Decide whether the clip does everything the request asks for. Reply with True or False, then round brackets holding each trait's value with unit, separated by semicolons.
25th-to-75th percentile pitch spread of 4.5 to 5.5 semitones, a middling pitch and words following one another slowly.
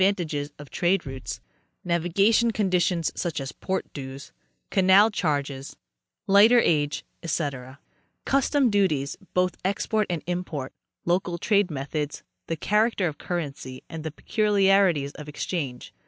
True (5.2 semitones; 170 Hz; 120 wpm)